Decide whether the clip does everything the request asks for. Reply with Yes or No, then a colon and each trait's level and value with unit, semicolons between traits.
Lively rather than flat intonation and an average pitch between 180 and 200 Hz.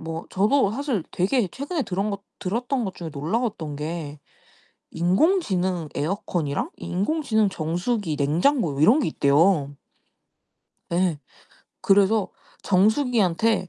Yes: wide, 5.8 semitones; high, 190 Hz